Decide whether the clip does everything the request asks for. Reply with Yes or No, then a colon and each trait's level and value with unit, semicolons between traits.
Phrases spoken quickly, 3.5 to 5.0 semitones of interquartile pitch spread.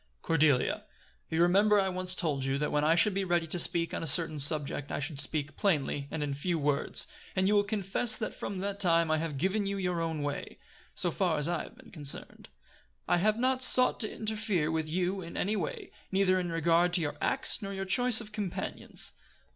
Yes: fast, 220 wpm; average, 4.3 semitones